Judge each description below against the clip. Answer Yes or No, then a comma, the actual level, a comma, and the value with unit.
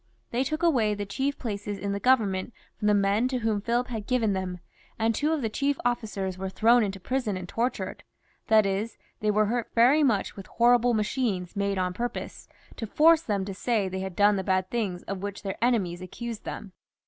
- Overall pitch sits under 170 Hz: No, high, 210 Hz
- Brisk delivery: Yes, fast, 210 wpm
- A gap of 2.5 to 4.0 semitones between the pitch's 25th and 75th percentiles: Yes, average, 3.6 semitones